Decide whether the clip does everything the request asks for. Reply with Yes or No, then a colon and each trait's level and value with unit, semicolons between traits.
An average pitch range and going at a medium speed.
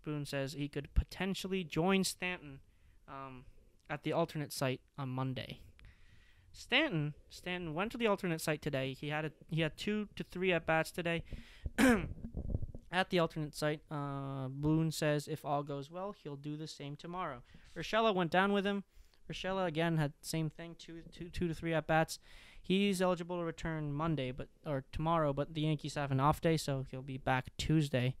Yes: average, 3.9 semitones; average, 185 wpm